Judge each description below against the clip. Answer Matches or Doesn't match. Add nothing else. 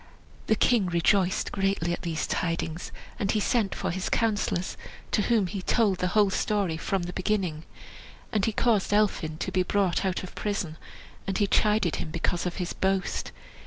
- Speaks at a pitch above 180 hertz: Matches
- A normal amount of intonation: Matches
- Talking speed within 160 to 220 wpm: Matches